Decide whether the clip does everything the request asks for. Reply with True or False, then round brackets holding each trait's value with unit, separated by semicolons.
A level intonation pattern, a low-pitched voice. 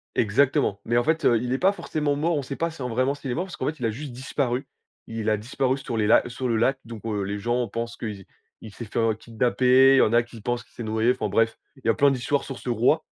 False (3.2 semitones; 120 Hz)